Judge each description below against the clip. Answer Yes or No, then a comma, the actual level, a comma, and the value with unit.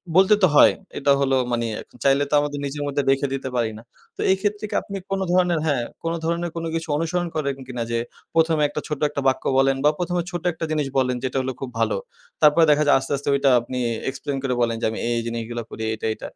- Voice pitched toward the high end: No, medium, 140 Hz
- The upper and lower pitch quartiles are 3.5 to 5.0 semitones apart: Yes, average, 4.0 semitones